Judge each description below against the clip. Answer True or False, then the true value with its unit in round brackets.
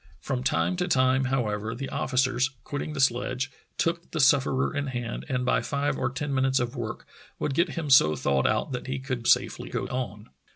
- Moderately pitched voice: False (130 Hz)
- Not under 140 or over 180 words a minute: False (200 wpm)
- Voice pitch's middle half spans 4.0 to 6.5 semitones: False (2.4 semitones)